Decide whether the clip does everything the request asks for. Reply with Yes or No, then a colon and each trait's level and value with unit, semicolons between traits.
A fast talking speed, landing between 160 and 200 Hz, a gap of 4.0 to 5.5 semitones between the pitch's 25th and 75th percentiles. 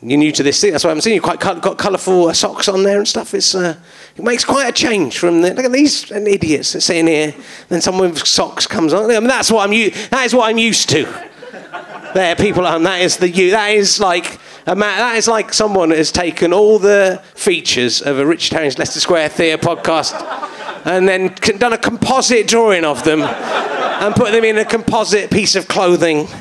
Yes: fast, 230 wpm; high, 190 Hz; average, 4.4 semitones